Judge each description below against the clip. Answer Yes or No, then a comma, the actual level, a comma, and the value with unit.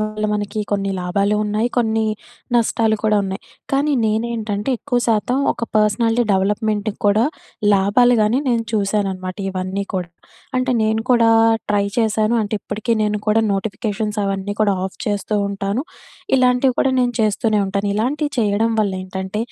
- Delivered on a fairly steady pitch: Yes, narrow, 2.2 semitones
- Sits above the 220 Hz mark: No, high, 215 Hz